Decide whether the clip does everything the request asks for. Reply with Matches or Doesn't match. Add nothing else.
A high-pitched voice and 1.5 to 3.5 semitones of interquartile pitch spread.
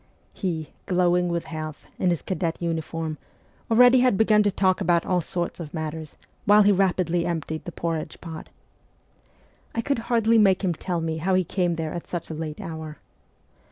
Doesn't match